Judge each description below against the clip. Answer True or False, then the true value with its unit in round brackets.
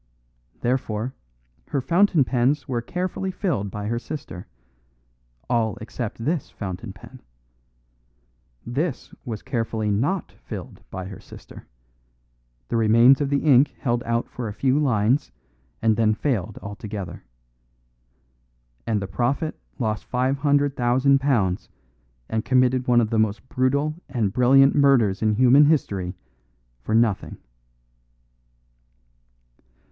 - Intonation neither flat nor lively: True (4.2 semitones)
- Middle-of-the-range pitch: False (120 Hz)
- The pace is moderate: False (120 wpm)